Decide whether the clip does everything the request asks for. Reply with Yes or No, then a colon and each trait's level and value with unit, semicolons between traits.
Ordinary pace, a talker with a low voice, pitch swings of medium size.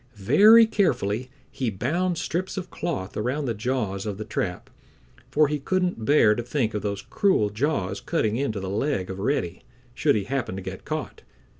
No: average, 180 wpm; low, 120 Hz; wide, 6.9 semitones